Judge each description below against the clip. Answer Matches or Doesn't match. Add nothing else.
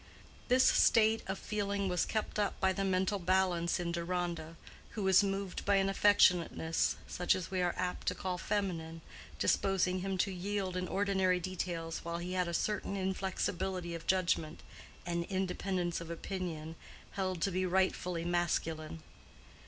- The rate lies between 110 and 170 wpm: Matches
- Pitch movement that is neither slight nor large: Doesn't match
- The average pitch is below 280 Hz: Matches